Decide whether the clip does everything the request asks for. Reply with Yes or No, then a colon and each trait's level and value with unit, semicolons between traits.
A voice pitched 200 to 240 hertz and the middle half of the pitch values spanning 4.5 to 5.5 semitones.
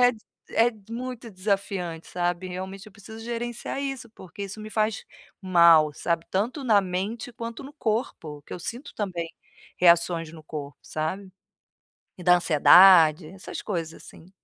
No: high, 190 Hz; average, 4.8 semitones